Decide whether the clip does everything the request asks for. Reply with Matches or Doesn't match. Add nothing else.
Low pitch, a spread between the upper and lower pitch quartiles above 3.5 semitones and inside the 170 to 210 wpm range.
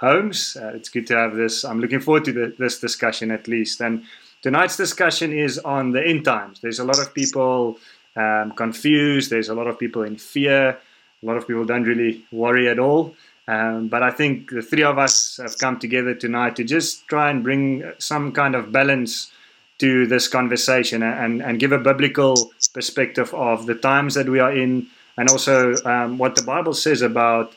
Doesn't match